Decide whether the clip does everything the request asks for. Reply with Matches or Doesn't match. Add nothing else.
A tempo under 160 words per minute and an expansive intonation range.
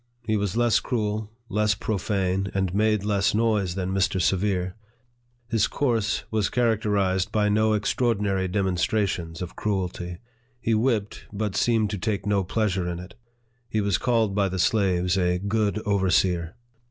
Doesn't match